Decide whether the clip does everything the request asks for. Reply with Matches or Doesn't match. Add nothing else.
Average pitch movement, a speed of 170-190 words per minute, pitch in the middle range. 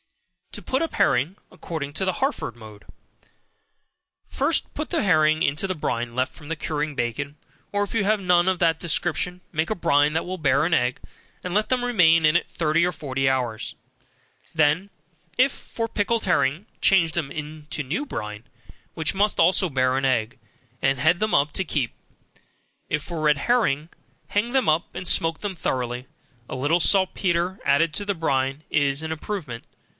Matches